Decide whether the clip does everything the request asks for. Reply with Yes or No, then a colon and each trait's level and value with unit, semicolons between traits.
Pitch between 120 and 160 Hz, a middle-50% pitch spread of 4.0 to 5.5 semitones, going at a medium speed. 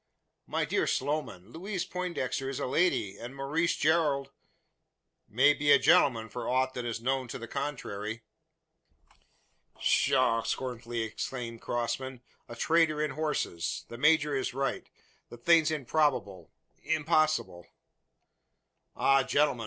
No: low, 135 Hz; average, 4.5 semitones; slow, 130 wpm